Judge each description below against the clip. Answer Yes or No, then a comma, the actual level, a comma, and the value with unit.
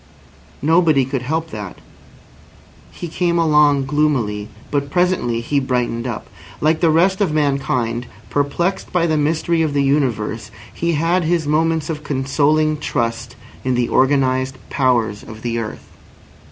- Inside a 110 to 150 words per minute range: Yes, average, 140 wpm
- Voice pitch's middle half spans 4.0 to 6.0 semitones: Yes, average, 4.4 semitones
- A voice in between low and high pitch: Yes, medium, 145 Hz